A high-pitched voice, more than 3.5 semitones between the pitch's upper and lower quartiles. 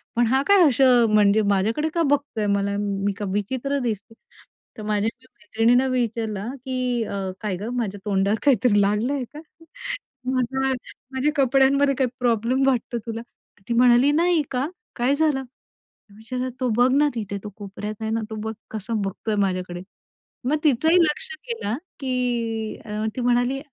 Yes: high, 240 Hz; average, 4.1 semitones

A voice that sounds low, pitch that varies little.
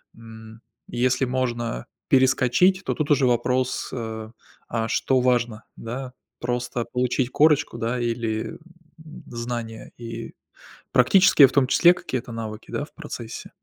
Yes: low, 125 Hz; narrow, 2.2 semitones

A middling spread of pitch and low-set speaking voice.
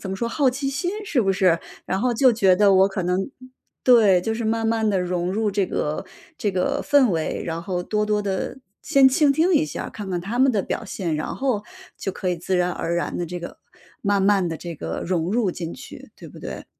No: average, 4.4 semitones; high, 200 Hz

